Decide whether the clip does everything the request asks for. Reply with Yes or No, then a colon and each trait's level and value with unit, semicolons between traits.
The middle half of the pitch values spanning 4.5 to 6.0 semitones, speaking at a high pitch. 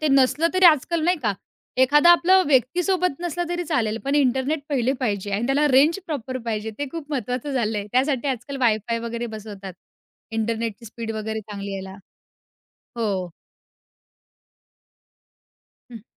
Yes: average, 5.2 semitones; very high, 255 Hz